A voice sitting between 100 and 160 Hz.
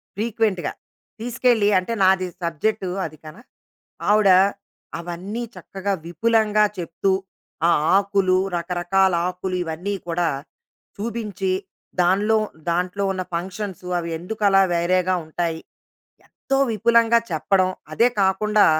No: high, 190 Hz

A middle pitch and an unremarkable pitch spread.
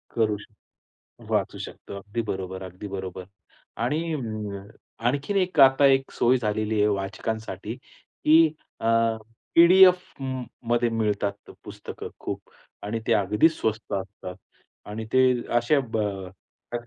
No: low, 110 Hz; average, 4.7 semitones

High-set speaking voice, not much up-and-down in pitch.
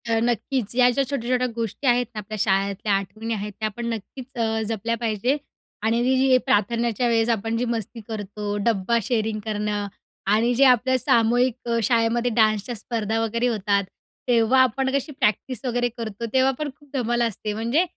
Yes: high, 230 Hz; narrow, 2.3 semitones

